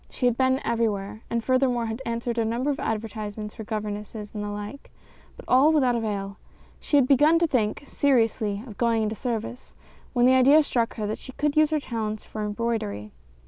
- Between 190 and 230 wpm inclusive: Yes, average, 195 wpm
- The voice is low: No, high, 230 Hz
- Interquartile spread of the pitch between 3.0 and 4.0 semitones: Yes, average, 3.5 semitones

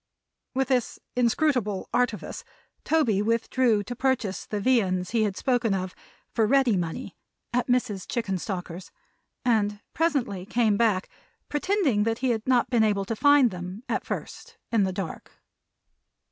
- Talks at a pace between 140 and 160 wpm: Yes, average, 145 wpm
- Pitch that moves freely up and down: No, average, 4.1 semitones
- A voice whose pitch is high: Yes, high, 225 Hz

